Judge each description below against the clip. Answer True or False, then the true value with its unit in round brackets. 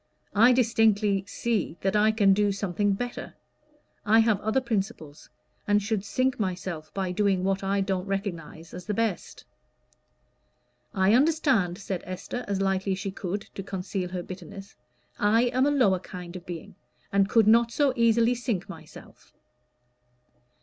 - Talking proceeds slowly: False (155 wpm)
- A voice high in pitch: True (200 Hz)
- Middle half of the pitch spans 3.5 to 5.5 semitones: False (3.0 semitones)